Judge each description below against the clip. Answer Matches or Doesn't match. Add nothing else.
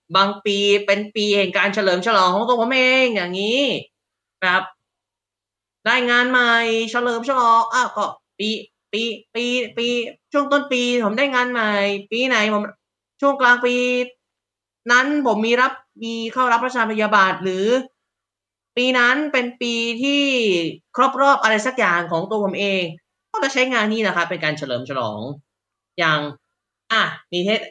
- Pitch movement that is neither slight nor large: Matches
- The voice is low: Doesn't match